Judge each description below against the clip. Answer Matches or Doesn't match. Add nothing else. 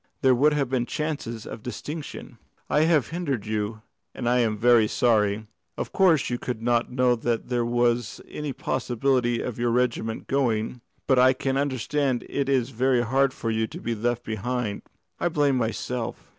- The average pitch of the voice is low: Matches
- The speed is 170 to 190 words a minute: Matches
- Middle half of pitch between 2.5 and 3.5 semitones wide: Matches